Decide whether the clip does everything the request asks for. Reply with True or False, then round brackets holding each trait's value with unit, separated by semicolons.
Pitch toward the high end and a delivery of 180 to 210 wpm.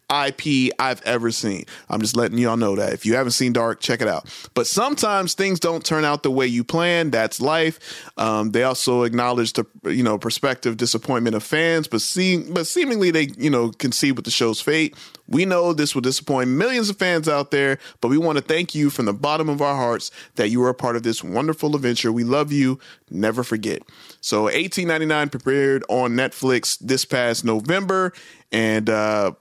False (135 Hz; 200 wpm)